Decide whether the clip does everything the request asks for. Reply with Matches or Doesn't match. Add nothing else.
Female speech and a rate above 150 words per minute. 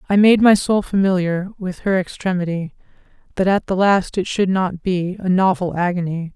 Matches